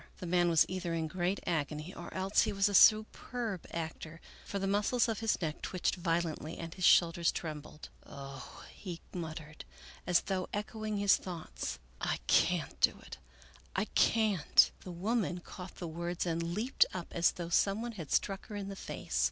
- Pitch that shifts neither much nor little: Yes, average, 3.3 semitones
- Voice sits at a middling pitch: Yes, medium, 180 Hz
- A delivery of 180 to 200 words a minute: Yes, average, 195 wpm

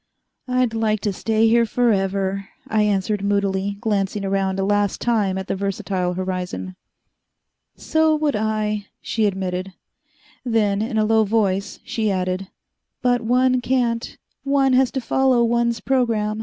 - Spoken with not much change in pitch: No, average, 3.3 semitones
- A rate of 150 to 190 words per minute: No, average, 140 wpm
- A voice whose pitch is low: No, high, 215 Hz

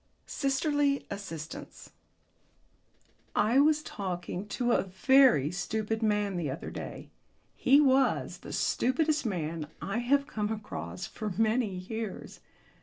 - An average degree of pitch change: No, wide, 6.4 semitones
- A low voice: No, high, 220 Hz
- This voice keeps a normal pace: No, slow, 115 wpm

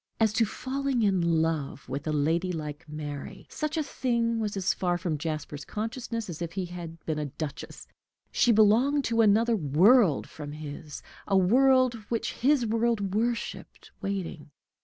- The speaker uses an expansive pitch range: Yes, wide, 6.6 semitones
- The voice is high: Yes, high, 195 Hz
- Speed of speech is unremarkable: Yes, average, 160 wpm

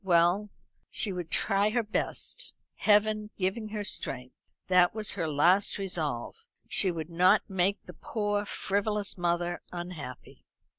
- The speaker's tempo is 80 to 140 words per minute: Yes, slow, 135 wpm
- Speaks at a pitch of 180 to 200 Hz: Yes, high, 190 Hz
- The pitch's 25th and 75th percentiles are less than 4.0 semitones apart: Yes, average, 3.2 semitones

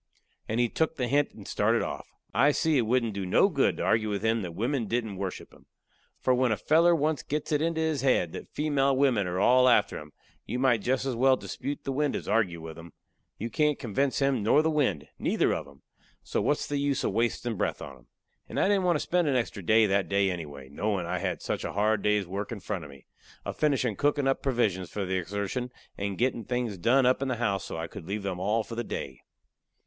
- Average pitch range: No, wide, 5.7 semitones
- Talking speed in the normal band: No, fast, 240 wpm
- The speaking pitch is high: No, low, 115 Hz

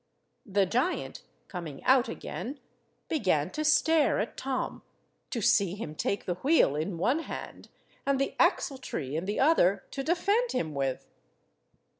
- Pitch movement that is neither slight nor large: No, wide, 8.4 semitones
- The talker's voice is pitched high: Yes, high, 230 Hz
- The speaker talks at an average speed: Yes, average, 145 wpm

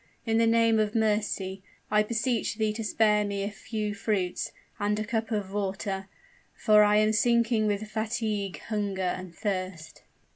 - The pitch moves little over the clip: Yes, narrow, 1.8 semitones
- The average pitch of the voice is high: Yes, high, 210 Hz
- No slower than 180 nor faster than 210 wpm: No, average, 160 wpm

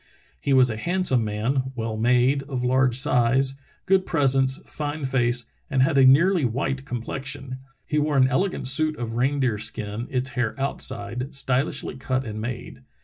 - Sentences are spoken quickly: No, average, 165 wpm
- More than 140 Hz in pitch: No, low, 130 Hz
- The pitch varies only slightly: Yes, narrow, 2.2 semitones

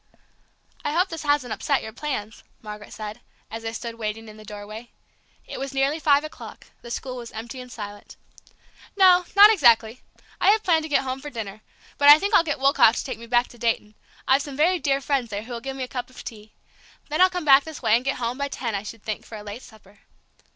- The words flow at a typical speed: No, fast, 235 wpm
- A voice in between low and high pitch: No, very high, 250 Hz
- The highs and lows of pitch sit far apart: No, average, 4.6 semitones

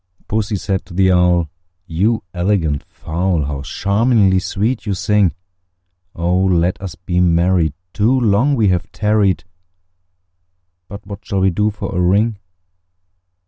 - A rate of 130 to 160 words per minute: Yes, average, 140 wpm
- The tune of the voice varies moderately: Yes, average, 3.0 semitones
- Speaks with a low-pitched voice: Yes, very low, 95 Hz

